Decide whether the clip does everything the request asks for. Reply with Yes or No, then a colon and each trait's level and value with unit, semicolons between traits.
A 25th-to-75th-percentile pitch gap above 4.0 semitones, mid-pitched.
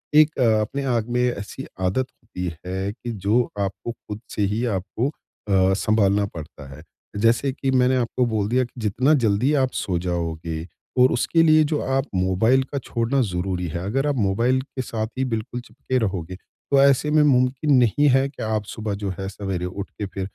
No: average, 5.1 semitones; low, 115 Hz